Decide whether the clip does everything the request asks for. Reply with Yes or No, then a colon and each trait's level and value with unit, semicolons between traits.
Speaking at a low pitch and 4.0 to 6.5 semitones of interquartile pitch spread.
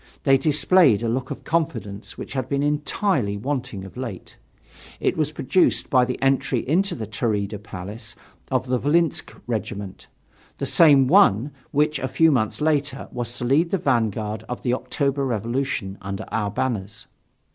Yes: low, 130 Hz; average, 5.2 semitones